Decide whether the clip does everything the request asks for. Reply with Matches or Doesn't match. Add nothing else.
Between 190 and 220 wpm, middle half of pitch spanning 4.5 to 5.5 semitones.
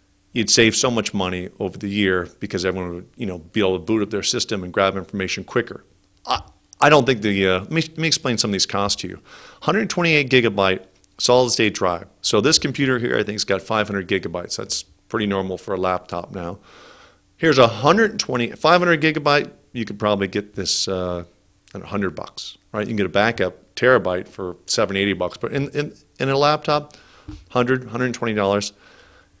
Matches